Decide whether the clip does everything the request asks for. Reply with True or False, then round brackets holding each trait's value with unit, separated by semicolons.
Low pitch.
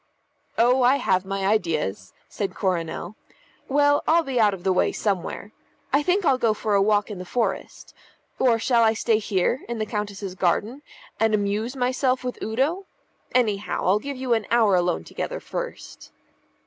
False (220 Hz)